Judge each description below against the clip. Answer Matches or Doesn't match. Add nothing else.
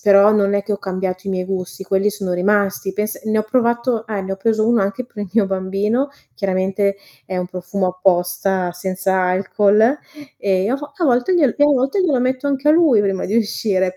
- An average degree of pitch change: Matches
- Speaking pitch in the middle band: Doesn't match